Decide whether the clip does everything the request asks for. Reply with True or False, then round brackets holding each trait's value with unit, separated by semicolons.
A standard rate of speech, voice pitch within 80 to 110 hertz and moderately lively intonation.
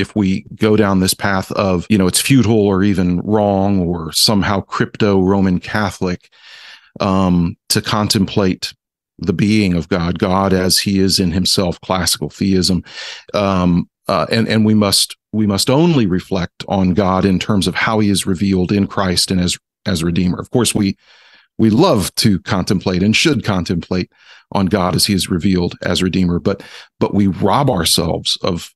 False (175 wpm; 95 Hz; 2.3 semitones)